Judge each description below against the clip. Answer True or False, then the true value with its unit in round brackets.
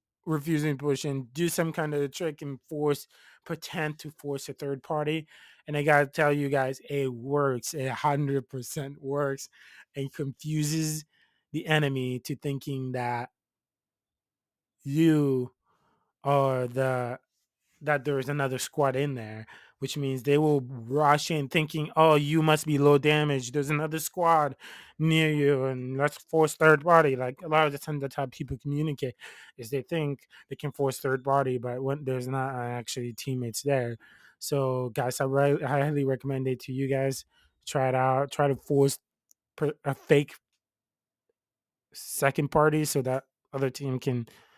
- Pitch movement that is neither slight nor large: False (2.3 semitones)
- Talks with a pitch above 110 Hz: True (140 Hz)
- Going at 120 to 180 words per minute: True (165 wpm)